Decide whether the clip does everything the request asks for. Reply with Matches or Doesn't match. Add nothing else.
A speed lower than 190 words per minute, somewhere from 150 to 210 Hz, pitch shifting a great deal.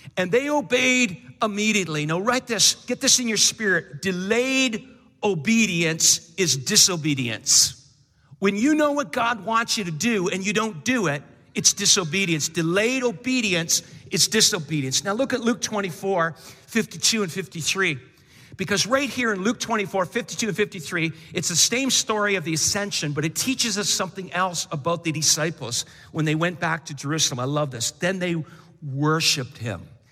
Matches